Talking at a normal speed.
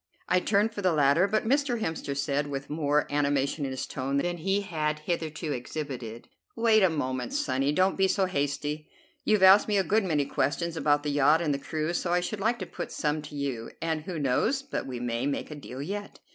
No: fast, 225 wpm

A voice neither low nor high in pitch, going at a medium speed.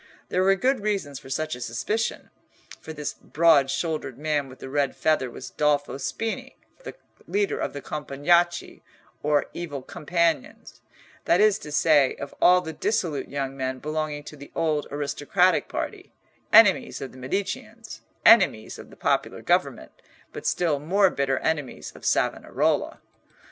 Yes: medium, 150 Hz; average, 150 wpm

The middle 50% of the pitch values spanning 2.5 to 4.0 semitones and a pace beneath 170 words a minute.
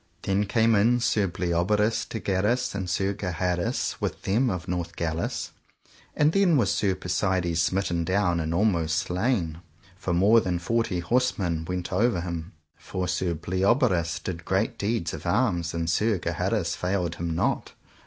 Yes: average, 3.5 semitones; average, 155 wpm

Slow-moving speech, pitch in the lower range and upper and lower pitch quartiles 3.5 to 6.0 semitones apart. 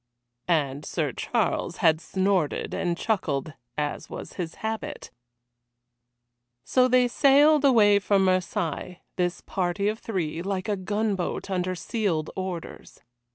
No: slow, 120 wpm; high, 190 Hz; average, 4.0 semitones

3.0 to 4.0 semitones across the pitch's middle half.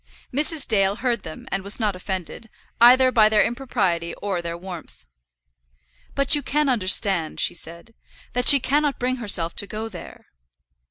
No: wide, 5.6 semitones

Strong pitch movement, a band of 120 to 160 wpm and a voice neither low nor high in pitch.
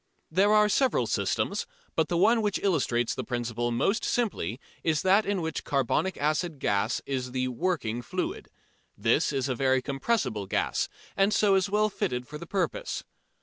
No: wide, 7.8 semitones; average, 170 wpm; medium, 155 Hz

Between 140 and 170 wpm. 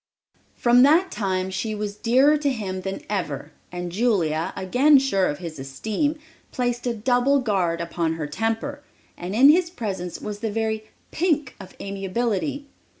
Yes: average, 155 wpm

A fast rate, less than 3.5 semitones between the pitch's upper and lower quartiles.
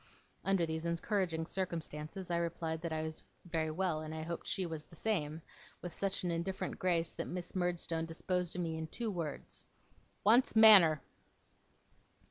No: average, 170 wpm; narrow, 2.5 semitones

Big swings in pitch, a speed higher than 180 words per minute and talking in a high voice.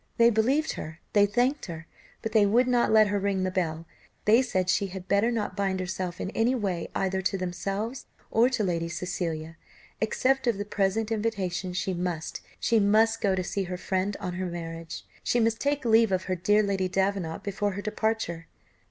No: average, 3.4 semitones; average, 195 wpm; high, 200 Hz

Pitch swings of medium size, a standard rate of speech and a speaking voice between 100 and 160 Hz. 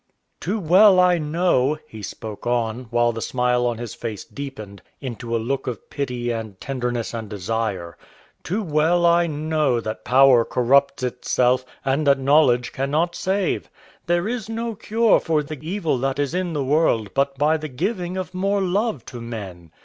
No: wide, 6.3 semitones; average, 170 wpm; medium, 140 Hz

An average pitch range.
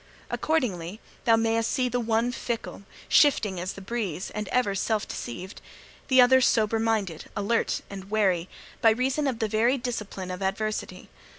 Yes: average, 3.6 semitones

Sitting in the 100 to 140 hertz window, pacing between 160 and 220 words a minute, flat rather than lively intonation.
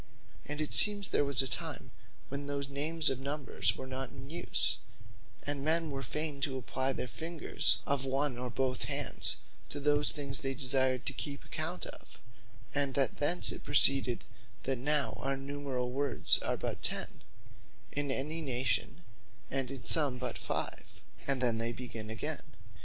Yes: low, 135 Hz; average, 170 wpm; narrow, 2.0 semitones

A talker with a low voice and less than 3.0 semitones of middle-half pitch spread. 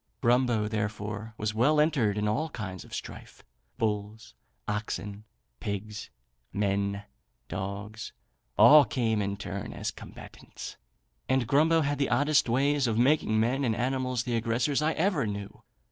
No: low, 110 Hz; average, 4.4 semitones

